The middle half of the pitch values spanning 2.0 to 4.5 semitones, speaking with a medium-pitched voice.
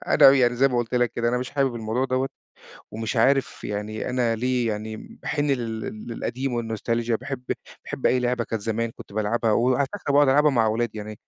No: narrow, 2.4 semitones; low, 120 Hz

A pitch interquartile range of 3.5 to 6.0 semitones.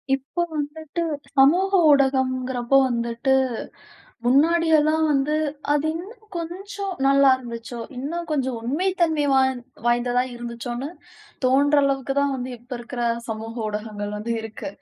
Yes: average, 4.1 semitones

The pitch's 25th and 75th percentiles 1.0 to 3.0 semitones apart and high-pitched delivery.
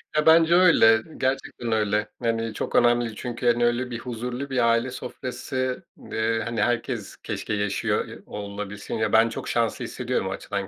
No: narrow, 2.4 semitones; low, 115 Hz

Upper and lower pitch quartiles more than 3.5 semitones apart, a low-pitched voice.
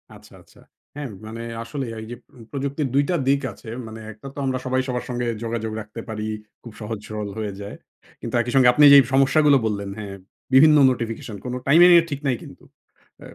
Yes: average, 4.0 semitones; low, 125 Hz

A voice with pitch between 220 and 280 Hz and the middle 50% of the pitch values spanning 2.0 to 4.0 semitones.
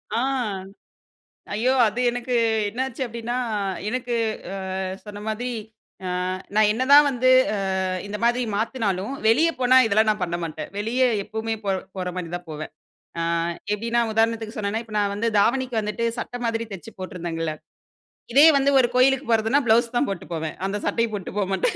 Yes: high, 225 Hz; average, 3.3 semitones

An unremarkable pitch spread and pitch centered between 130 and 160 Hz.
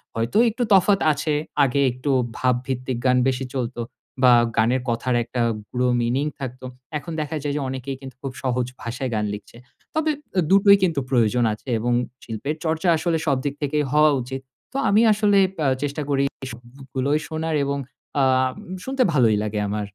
Yes: average, 3.7 semitones; low, 135 Hz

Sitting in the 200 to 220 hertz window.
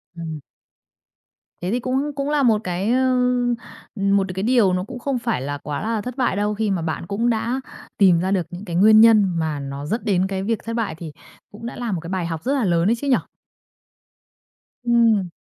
Yes: high, 205 Hz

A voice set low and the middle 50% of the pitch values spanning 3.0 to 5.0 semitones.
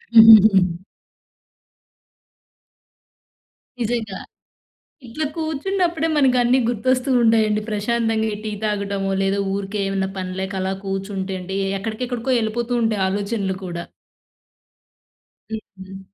No: high, 215 Hz; average, 3.5 semitones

